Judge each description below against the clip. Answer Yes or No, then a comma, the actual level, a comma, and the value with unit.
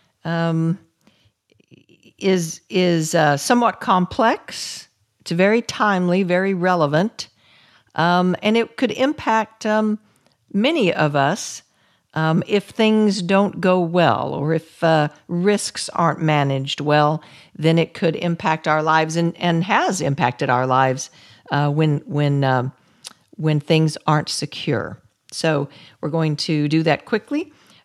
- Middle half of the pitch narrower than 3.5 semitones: No, average, 4.3 semitones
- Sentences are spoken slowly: Yes, slow, 130 wpm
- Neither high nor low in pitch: Yes, medium, 165 Hz